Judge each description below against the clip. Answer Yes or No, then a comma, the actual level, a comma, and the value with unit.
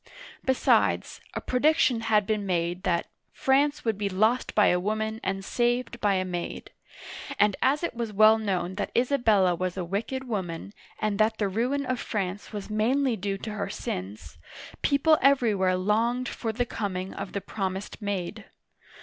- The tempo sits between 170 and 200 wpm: Yes, average, 175 wpm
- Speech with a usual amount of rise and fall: Yes, average, 4.1 semitones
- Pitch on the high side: Yes, high, 215 Hz